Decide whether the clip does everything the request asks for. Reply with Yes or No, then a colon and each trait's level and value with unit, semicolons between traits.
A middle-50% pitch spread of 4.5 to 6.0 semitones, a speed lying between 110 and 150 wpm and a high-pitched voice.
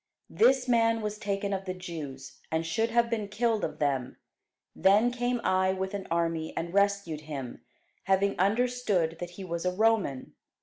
No: average, 5.0 semitones; average, 170 wpm; high, 195 Hz